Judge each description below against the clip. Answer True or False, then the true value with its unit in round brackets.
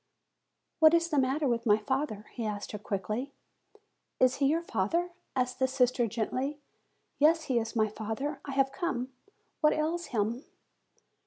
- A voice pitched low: False (260 Hz)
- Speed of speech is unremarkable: True (160 wpm)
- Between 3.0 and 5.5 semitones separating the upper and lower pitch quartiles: True (5.1 semitones)